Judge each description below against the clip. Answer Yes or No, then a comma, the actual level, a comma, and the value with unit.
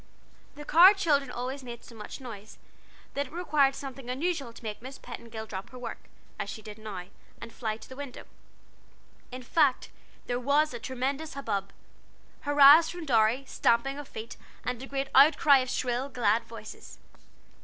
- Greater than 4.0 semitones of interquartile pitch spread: No, average, 3.5 semitones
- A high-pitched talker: Yes, very high, 255 Hz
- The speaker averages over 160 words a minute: Yes, average, 170 wpm